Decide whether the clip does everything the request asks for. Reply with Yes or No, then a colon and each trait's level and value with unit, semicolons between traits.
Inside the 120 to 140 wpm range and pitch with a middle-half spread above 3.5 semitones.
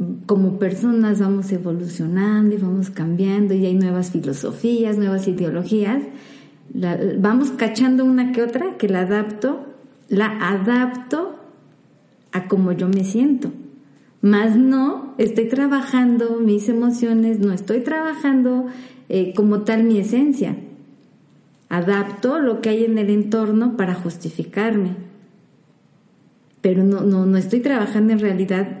Yes: slow, 125 wpm; average, 4.5 semitones